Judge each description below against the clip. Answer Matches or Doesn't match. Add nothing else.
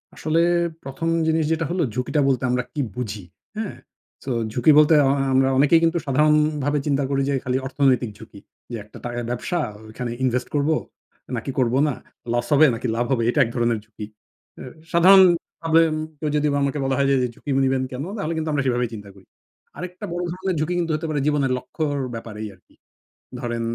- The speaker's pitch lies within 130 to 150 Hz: Matches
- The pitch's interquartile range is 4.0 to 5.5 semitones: Matches